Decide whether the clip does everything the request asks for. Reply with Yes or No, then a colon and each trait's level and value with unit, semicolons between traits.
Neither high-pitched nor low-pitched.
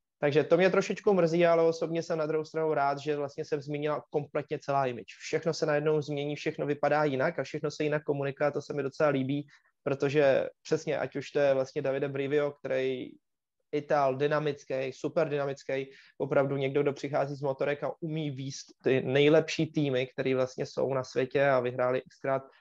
Yes: medium, 145 Hz